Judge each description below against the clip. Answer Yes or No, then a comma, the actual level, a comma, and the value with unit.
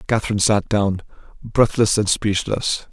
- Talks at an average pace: No, slow, 125 wpm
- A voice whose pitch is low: Yes, low, 105 Hz